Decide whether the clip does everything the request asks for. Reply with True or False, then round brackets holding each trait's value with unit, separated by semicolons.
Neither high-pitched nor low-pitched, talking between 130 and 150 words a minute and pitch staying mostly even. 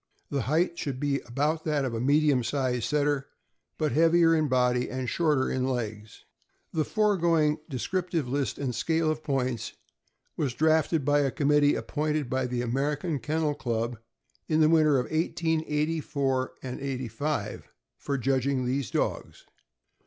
False (145 Hz; 145 wpm; 3.3 semitones)